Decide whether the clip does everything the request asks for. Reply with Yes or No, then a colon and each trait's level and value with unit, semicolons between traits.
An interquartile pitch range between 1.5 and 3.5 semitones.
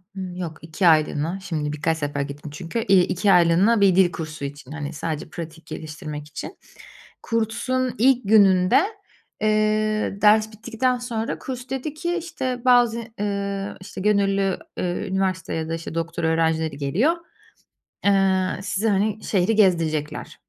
No: average, 5.0 semitones